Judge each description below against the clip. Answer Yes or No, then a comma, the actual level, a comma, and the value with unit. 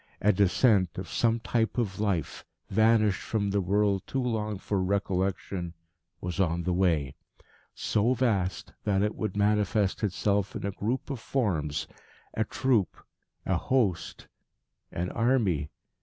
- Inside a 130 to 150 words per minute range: Yes, average, 140 wpm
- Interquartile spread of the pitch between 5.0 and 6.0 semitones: No, average, 3.2 semitones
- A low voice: Yes, low, 100 Hz